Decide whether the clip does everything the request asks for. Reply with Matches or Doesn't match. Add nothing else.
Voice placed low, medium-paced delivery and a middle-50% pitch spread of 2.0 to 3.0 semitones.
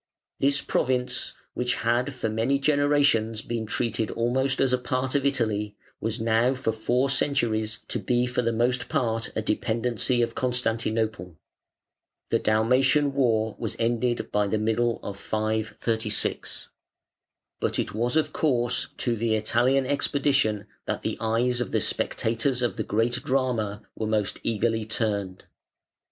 Matches